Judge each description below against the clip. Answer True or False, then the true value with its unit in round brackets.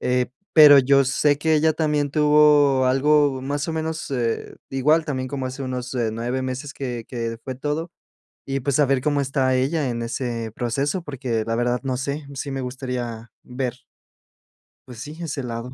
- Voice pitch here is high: False (135 Hz)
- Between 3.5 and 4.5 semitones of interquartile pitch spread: False (2.8 semitones)